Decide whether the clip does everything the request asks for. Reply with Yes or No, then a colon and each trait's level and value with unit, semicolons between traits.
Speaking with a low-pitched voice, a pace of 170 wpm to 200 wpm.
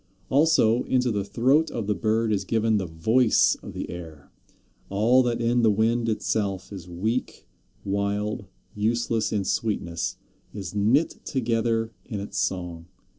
No: low, 110 Hz; average, 145 wpm